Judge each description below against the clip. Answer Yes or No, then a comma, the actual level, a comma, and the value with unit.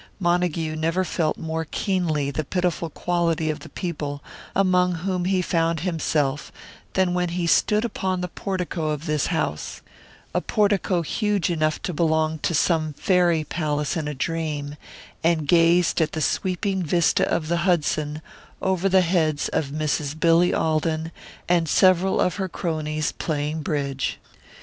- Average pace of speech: Yes, average, 150 wpm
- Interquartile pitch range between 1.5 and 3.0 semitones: Yes, narrow, 2.6 semitones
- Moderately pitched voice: Yes, medium, 165 Hz